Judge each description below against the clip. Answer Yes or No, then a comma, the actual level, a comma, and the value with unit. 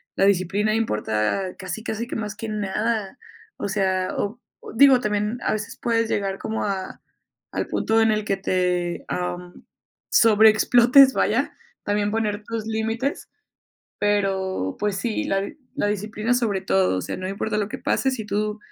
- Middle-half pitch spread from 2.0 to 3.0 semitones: Yes, narrow, 2.5 semitones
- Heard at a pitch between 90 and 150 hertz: No, high, 210 Hz